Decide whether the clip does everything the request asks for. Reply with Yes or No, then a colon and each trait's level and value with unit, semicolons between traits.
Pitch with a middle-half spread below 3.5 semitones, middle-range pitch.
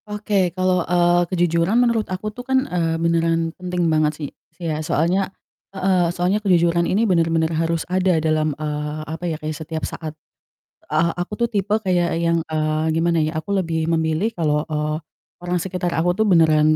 Yes: narrow, 2.5 semitones; medium, 170 Hz